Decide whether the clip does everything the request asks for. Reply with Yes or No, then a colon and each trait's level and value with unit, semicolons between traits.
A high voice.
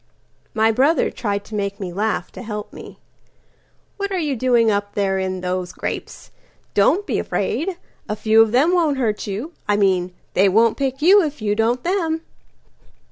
Yes: high, 220 Hz